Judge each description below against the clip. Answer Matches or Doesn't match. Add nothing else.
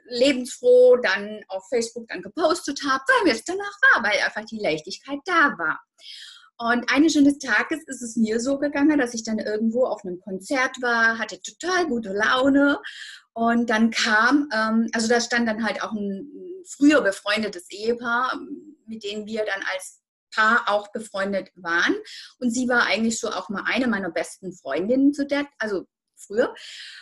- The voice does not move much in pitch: Doesn't match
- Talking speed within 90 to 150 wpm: Doesn't match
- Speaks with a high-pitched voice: Matches